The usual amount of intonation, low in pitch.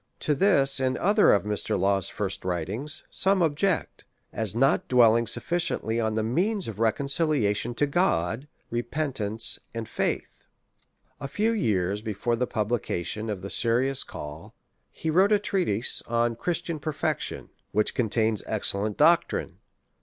No: wide, 6.4 semitones; low, 120 Hz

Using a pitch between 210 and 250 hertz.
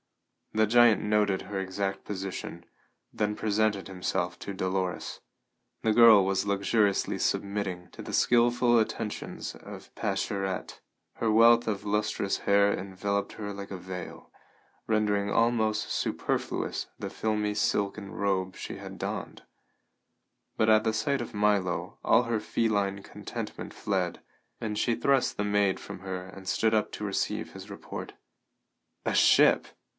No: low, 105 Hz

